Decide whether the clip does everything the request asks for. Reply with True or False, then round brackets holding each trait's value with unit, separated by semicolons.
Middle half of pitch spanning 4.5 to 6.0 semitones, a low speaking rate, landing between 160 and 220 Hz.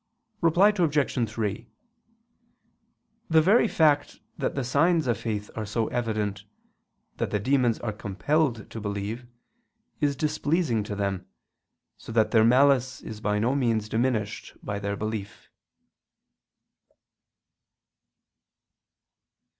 False (5.2 semitones; 115 wpm; 115 Hz)